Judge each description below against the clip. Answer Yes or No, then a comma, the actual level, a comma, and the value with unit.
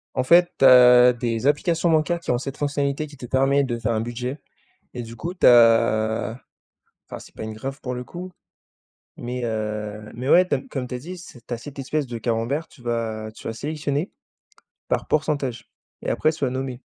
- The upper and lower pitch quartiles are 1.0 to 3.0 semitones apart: No, average, 3.8 semitones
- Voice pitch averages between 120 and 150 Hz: Yes, low, 125 Hz